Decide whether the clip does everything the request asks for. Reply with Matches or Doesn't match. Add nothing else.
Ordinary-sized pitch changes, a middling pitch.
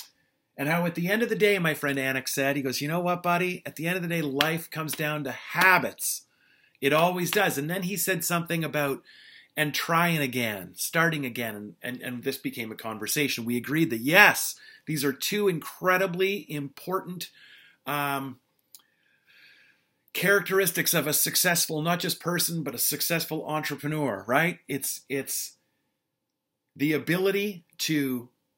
Matches